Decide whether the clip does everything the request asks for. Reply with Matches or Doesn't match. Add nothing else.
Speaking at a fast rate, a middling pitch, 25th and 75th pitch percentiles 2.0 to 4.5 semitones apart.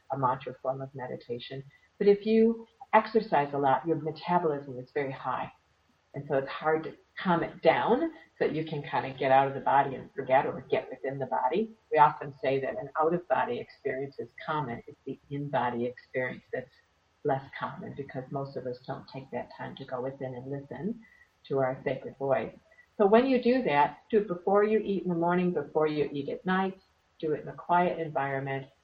Doesn't match